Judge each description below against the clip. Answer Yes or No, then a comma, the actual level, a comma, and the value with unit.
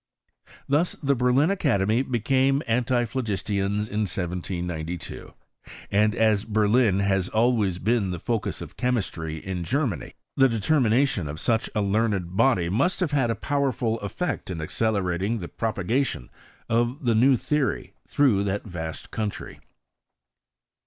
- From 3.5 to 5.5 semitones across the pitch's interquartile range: Yes, average, 4.7 semitones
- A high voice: No, low, 110 Hz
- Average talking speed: No, slow, 130 wpm